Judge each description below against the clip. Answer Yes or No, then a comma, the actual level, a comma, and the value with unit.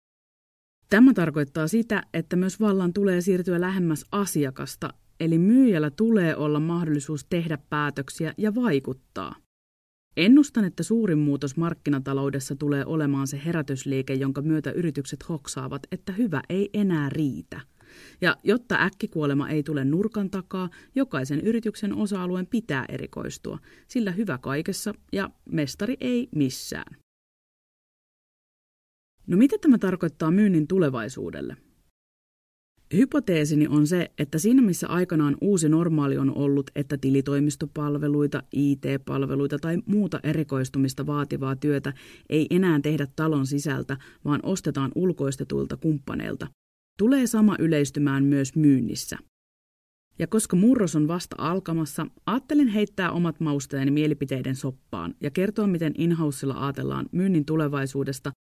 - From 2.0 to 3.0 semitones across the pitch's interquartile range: No, average, 5.1 semitones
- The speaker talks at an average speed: Yes, average, 115 wpm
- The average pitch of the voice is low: No, medium, 155 Hz